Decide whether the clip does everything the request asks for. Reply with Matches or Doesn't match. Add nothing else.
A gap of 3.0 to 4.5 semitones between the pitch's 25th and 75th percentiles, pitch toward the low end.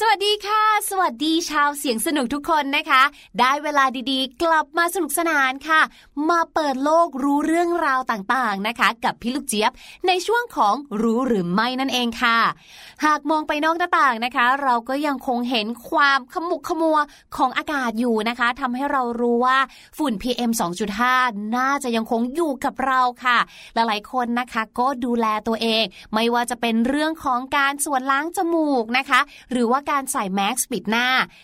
Doesn't match